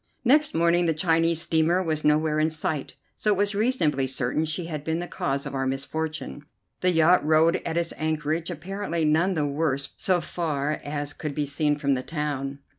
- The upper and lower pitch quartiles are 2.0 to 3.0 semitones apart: Yes, narrow, 2.5 semitones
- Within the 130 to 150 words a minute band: No, average, 190 wpm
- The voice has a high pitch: No, medium, 155 Hz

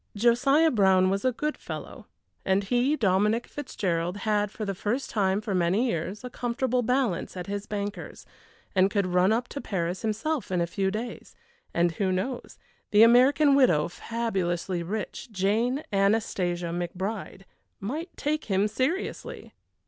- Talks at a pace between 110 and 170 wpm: Yes, average, 150 wpm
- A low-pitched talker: No, high, 205 Hz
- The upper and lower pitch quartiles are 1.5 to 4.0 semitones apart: No, average, 4.6 semitones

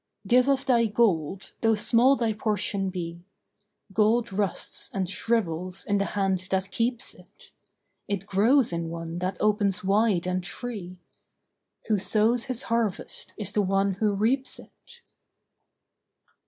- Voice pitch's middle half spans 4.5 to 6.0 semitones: No, average, 3.7 semitones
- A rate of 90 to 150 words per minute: Yes, average, 140 wpm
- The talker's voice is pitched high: Yes, high, 205 Hz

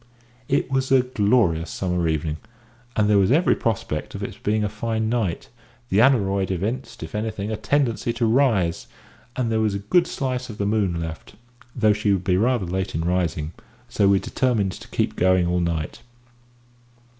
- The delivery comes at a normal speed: Yes, average, 180 wpm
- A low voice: Yes, low, 105 Hz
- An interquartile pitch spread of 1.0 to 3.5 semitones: No, average, 4.5 semitones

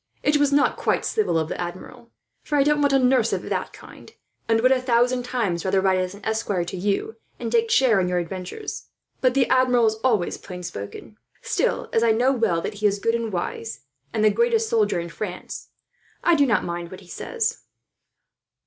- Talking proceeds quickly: Yes, fast, 210 wpm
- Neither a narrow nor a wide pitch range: No, wide, 6.3 semitones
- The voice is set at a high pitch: Yes, high, 225 Hz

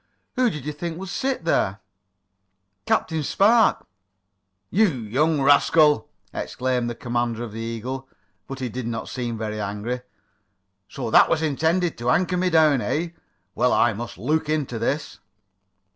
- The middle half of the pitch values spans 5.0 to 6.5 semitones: Yes, wide, 5.4 semitones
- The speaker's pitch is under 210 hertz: Yes, low, 135 Hz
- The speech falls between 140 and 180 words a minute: Yes, average, 150 wpm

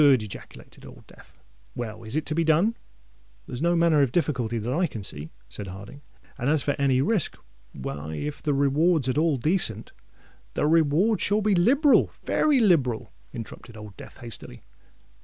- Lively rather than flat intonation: Yes, wide, 6.8 semitones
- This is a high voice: No, medium, 140 Hz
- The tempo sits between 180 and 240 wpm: No, average, 160 wpm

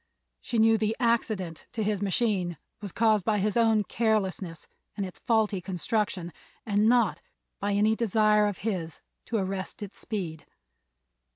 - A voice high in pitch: Yes, high, 210 Hz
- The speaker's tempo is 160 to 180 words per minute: No, average, 150 wpm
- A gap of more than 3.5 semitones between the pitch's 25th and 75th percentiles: No, average, 2.8 semitones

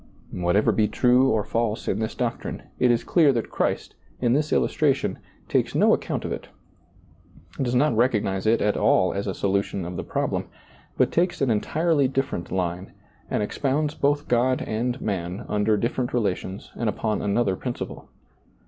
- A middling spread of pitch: Yes, average, 4.5 semitones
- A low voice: Yes, low, 115 Hz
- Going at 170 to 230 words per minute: Yes, average, 175 wpm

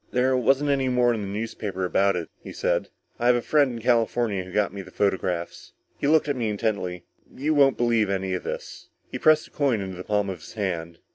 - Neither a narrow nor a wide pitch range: Yes, average, 4.9 semitones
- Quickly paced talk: Yes, fast, 230 wpm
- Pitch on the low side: Yes, low, 110 Hz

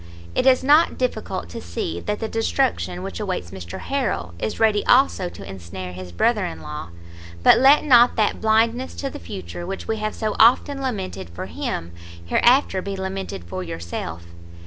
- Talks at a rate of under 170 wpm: No, average, 175 wpm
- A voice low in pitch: No, high, 190 Hz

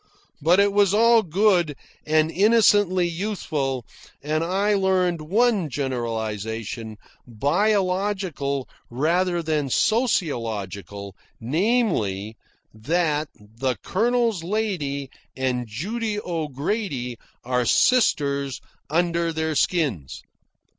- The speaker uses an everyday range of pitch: No, wide, 7.4 semitones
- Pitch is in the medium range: Yes, medium, 160 Hz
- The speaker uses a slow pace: Yes, slow, 85 wpm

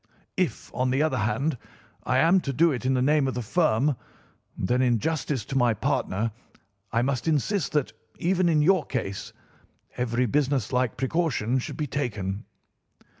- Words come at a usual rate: Yes, average, 165 wpm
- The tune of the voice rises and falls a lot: No, average, 3.9 semitones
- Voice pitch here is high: No, low, 130 Hz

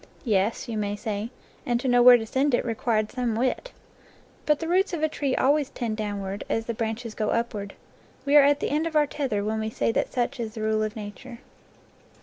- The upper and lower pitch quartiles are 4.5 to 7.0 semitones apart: No, average, 4.0 semitones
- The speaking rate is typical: No, fast, 230 wpm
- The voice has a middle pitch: No, high, 235 Hz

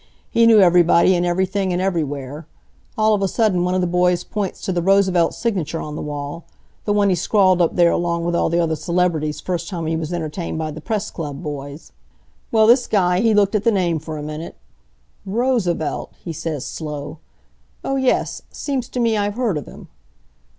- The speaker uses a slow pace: No, average, 200 wpm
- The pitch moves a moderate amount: Yes, average, 4.1 semitones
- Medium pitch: Yes, medium, 175 Hz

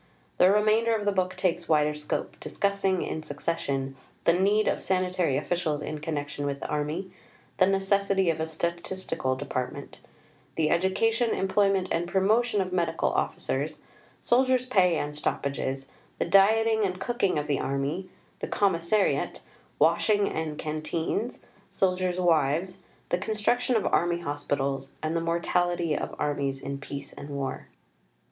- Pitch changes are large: No, average, 4.7 semitones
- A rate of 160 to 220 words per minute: No, average, 140 wpm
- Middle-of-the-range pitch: Yes, medium, 175 Hz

